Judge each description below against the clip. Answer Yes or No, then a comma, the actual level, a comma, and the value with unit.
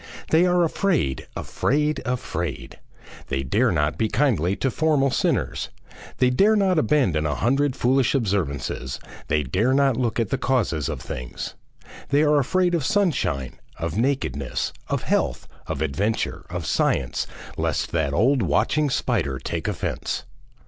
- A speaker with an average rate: Yes, average, 145 wpm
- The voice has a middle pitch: No, low, 125 Hz